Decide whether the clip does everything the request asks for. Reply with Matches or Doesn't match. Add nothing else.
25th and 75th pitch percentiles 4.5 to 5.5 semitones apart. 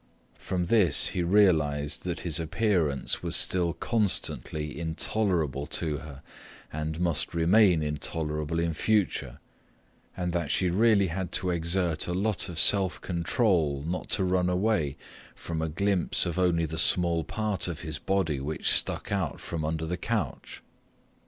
Doesn't match